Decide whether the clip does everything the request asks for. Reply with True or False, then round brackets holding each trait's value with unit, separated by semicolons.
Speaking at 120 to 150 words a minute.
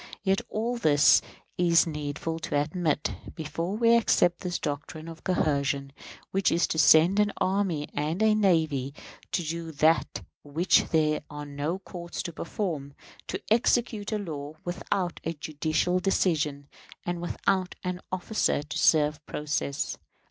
True (145 wpm)